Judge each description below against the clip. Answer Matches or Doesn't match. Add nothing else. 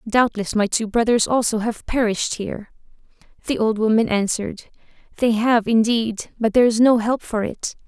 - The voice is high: Matches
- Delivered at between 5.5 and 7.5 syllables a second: Doesn't match